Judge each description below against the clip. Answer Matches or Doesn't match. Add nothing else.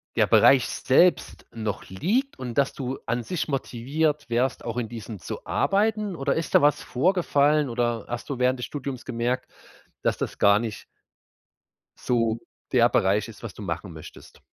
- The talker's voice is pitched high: Doesn't match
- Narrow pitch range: Doesn't match